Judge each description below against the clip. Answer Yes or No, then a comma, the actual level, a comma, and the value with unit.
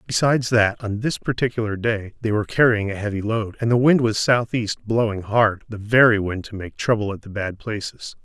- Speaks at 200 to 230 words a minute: Yes, fast, 205 wpm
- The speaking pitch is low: Yes, low, 110 Hz